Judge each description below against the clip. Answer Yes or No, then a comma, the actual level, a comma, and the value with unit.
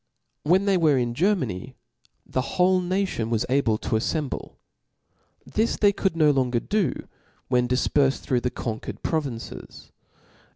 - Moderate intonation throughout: No, wide, 6.8 semitones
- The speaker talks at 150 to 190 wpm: No, average, 140 wpm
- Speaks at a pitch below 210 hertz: Yes, medium, 140 Hz